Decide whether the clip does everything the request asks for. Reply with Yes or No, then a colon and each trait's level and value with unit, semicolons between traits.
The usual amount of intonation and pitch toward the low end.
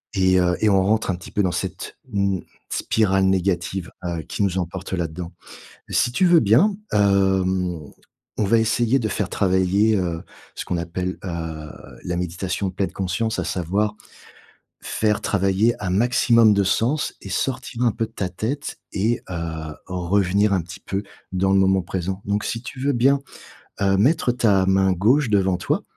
Yes: average, 3.2 semitones; very low, 95 Hz